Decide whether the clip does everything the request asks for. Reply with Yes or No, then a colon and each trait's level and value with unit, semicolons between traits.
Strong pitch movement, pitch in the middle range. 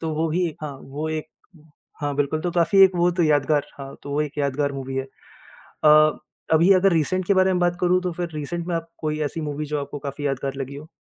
No: average, 3.5 semitones; medium, 155 Hz